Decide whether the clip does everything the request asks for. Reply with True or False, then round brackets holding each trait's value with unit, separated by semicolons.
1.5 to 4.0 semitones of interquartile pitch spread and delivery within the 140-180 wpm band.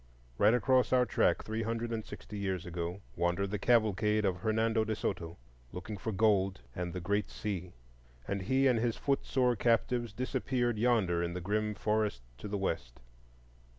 True (3.5 semitones; 175 wpm)